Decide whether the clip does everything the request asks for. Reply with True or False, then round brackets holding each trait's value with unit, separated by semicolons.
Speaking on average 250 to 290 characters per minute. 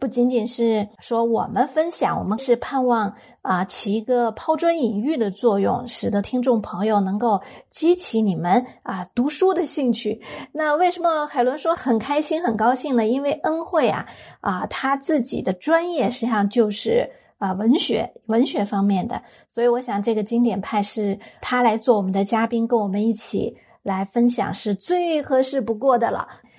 True (260 characters per minute)